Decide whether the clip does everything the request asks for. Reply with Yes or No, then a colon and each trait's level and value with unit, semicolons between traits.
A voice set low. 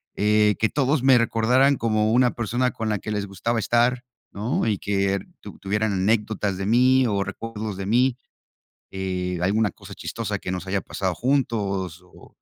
Yes: low, 110 Hz